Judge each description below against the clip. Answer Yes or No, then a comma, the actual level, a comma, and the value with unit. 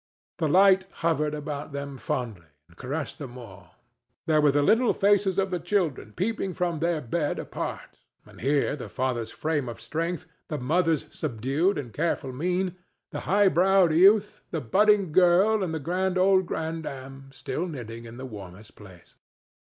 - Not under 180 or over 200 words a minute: No, average, 165 wpm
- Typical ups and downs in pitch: No, wide, 5.8 semitones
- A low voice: No, medium, 160 Hz